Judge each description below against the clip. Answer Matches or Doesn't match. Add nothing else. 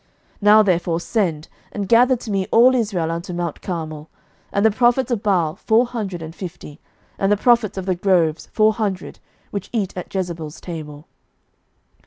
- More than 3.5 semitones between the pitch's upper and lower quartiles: Matches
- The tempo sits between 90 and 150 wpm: Doesn't match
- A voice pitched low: Doesn't match